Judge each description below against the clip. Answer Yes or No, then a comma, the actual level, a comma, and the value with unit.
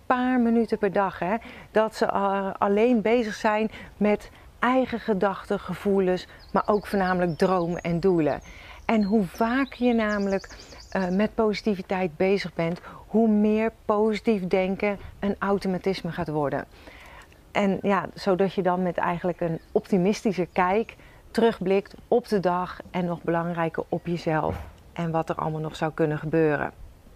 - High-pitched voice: Yes, high, 195 Hz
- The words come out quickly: No, average, 145 wpm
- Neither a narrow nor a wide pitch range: Yes, average, 3.7 semitones